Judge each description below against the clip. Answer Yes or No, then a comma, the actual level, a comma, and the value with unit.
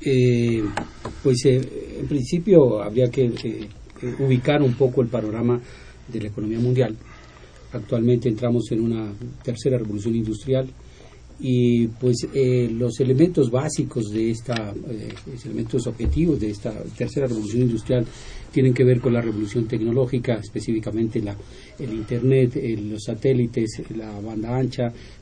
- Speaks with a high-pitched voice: No, low, 120 Hz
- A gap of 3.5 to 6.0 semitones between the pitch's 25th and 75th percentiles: No, average, 2.8 semitones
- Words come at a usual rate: Yes, average, 140 wpm